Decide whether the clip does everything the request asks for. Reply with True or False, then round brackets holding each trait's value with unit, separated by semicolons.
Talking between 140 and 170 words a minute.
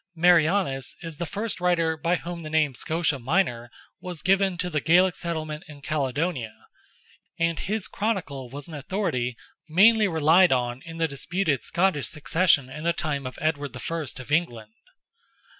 True (160 wpm)